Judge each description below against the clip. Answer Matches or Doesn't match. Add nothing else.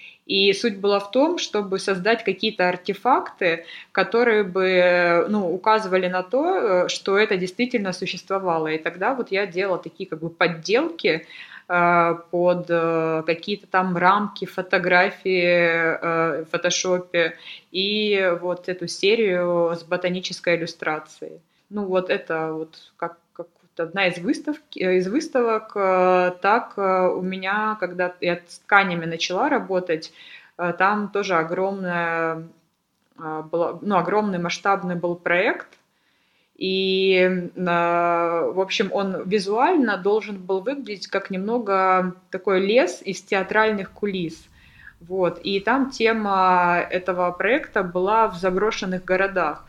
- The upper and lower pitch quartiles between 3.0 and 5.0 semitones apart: Doesn't match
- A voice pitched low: Doesn't match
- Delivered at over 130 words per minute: Doesn't match